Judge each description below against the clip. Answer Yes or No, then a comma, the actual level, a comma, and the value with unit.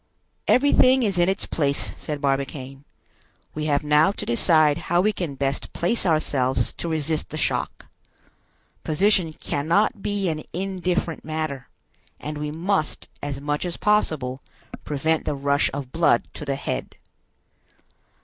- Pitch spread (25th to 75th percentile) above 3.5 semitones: Yes, average, 3.9 semitones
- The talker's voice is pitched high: No, medium, 155 Hz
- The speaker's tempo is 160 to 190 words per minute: No, average, 140 wpm